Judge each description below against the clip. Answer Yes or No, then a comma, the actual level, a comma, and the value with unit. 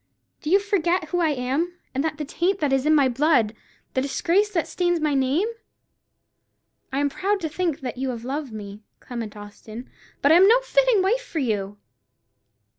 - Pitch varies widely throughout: Yes, wide, 5.7 semitones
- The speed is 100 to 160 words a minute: No, average, 190 wpm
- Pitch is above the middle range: Yes, very high, 300 Hz